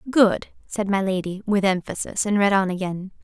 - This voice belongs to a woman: Yes, female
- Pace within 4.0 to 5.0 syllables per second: No, 5.2 syllables/s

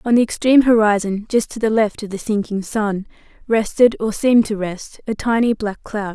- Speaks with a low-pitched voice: No, high, 215 Hz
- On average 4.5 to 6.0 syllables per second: Yes, 5.2 syllables/s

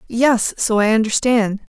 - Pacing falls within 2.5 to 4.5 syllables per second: Yes, 4.2 syllables/s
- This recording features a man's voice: No, female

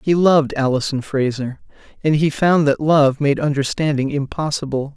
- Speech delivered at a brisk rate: No, average, 145 wpm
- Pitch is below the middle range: No, medium, 145 Hz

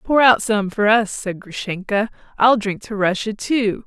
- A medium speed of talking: Yes, average, 185 wpm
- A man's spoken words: No, female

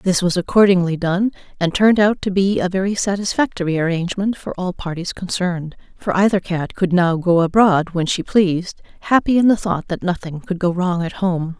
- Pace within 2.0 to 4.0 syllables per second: No, 5.3 syllables/s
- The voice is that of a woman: Yes, female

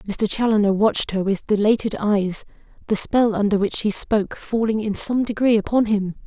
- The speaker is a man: No, female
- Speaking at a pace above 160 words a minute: Yes, average, 180 wpm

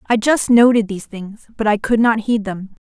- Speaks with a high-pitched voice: Yes, high, 220 Hz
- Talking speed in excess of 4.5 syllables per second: Yes, 5.1 syllables/s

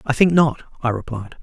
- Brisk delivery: Yes, fast, 210 wpm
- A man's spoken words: Yes, male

